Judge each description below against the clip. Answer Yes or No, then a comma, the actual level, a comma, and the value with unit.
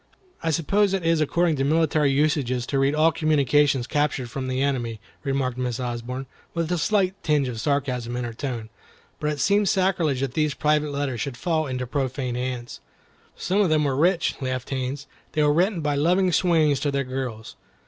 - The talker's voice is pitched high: No, medium, 140 Hz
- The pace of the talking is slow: No, average, 190 wpm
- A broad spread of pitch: No, average, 3.6 semitones